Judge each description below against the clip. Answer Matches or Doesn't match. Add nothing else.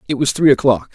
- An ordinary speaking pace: Doesn't match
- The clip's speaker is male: Matches